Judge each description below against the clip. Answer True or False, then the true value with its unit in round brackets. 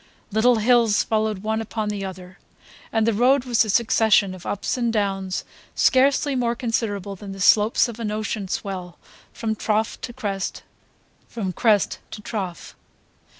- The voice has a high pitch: True (215 Hz)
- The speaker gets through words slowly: False (155 wpm)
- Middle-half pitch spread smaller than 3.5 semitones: True (2.8 semitones)